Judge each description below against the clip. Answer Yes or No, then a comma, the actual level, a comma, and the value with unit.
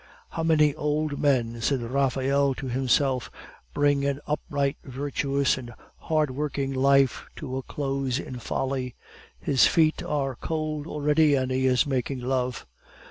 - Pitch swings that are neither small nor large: No, narrow, 2.1 semitones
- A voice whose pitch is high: No, medium, 140 Hz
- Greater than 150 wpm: No, average, 140 wpm